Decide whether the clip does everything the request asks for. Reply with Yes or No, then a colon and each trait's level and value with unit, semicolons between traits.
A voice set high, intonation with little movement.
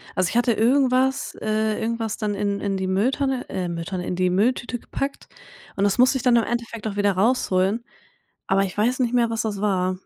No: high, 220 Hz; average, 3.7 semitones